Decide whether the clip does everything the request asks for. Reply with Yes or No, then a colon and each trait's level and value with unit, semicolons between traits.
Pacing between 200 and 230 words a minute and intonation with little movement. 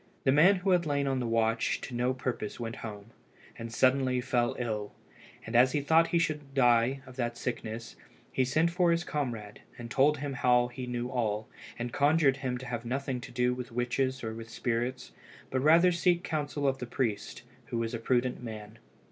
No: fast, 205 wpm; average, 3.0 semitones